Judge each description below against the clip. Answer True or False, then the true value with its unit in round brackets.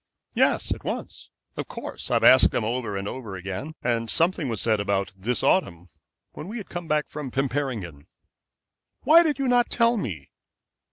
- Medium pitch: False (125 Hz)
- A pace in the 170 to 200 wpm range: True (175 wpm)